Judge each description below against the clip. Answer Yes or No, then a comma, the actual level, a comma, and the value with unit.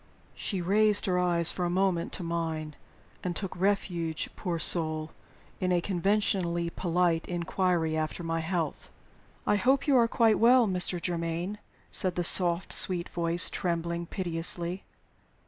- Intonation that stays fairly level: Yes, narrow, 2.3 semitones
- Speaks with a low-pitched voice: No, medium, 175 Hz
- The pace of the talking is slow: No, average, 145 wpm